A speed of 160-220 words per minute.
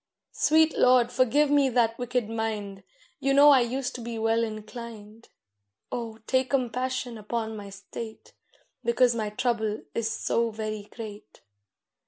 No: average, 140 wpm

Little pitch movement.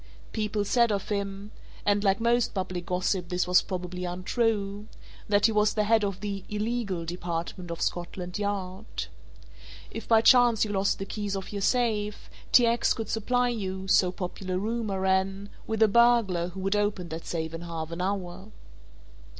No: average, 3.0 semitones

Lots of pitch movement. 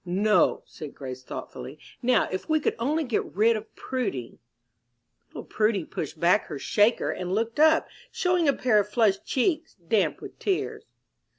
Yes: wide, 7.1 semitones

